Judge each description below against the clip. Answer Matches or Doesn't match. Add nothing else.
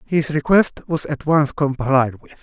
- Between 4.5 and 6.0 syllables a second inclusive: Doesn't match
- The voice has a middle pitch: Matches